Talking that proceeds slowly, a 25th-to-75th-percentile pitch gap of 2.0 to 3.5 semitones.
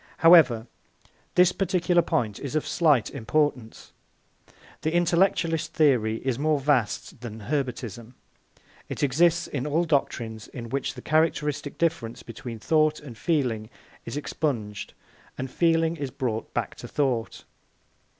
No: slow, 130 wpm; wide, 5.4 semitones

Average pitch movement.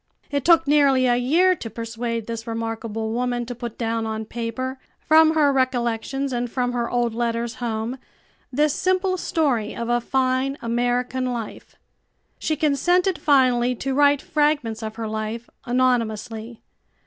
Yes: average, 3.2 semitones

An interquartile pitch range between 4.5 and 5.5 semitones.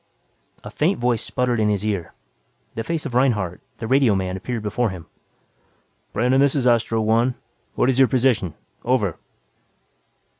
No: average, 3.6 semitones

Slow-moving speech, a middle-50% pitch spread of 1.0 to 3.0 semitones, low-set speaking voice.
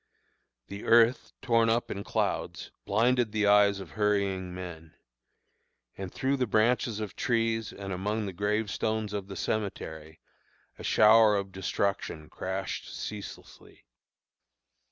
Yes: slow, 125 wpm; narrow, 2.6 semitones; low, 105 Hz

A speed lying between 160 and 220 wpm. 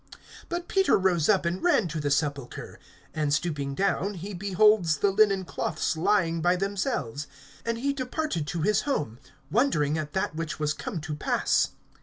Yes: average, 170 wpm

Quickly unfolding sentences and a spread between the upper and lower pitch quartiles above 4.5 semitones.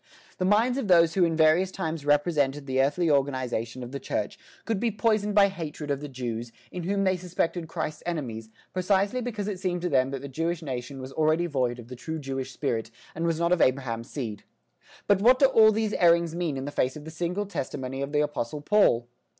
Yes: fast, 215 wpm; wide, 5.5 semitones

